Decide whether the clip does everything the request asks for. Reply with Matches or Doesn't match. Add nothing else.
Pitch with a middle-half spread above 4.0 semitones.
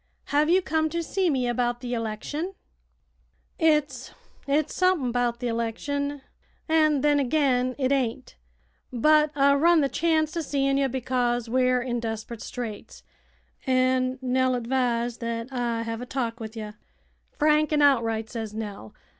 Doesn't match